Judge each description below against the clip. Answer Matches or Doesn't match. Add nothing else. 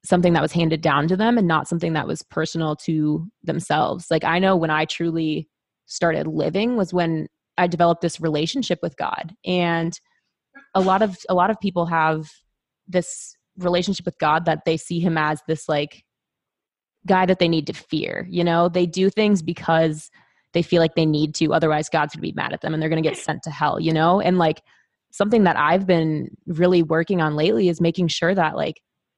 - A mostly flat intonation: Matches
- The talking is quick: Matches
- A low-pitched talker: Doesn't match